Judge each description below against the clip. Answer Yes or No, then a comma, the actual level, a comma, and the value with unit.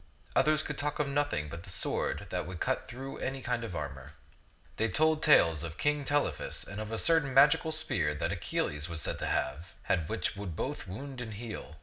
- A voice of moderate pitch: No, low, 115 Hz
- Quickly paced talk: Yes, fast, 210 wpm